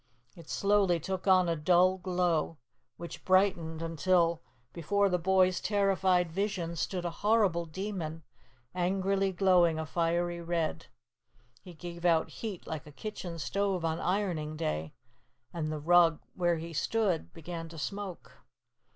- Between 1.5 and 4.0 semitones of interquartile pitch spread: Yes, narrow, 2.4 semitones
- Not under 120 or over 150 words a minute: Yes, average, 140 wpm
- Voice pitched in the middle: Yes, medium, 175 Hz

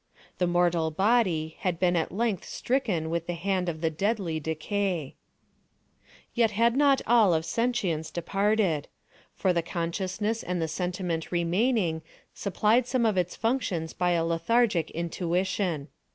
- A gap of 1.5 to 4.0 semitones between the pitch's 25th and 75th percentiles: No, average, 4.5 semitones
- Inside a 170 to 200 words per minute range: No, average, 140 wpm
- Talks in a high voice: No, medium, 180 Hz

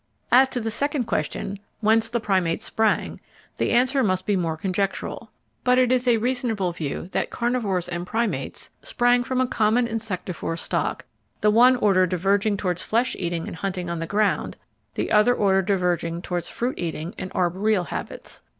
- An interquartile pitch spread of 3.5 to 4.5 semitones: No, average, 4.9 semitones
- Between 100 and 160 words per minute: No, average, 170 wpm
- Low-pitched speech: No, high, 205 Hz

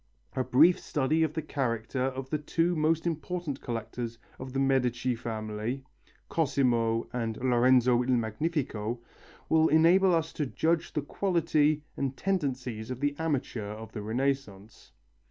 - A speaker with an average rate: Yes, average, 145 wpm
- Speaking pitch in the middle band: No, low, 130 Hz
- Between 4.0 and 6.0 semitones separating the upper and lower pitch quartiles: Yes, average, 5.0 semitones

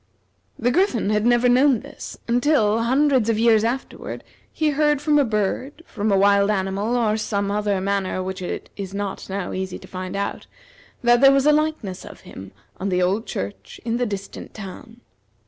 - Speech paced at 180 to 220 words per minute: Yes, average, 185 wpm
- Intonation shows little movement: No, average, 4.0 semitones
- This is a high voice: Yes, high, 215 Hz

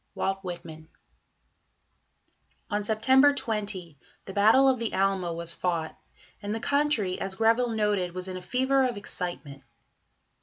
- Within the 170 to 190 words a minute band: No, average, 140 wpm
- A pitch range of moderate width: Yes, average, 4.3 semitones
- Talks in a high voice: Yes, high, 205 Hz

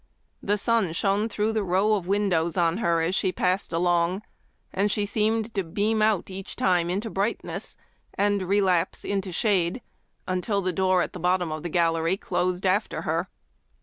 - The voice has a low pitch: No, high, 190 Hz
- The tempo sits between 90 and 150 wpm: No, average, 175 wpm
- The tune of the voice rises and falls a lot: No, average, 2.8 semitones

